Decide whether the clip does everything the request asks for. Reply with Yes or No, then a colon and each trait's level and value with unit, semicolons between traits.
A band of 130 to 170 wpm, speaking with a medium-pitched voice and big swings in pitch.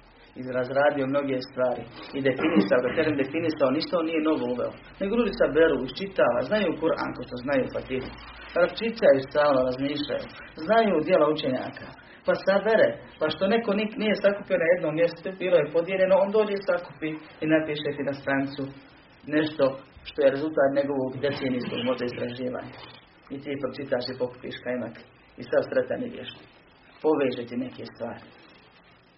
Yes: average, 150 wpm; medium, 145 Hz; wide, 5.7 semitones